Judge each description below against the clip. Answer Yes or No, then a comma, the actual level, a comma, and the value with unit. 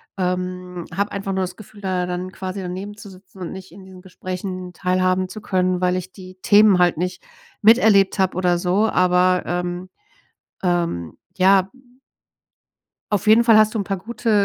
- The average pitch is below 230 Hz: Yes, medium, 185 Hz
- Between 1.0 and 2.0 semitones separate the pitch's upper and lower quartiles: Yes, narrow, 1.5 semitones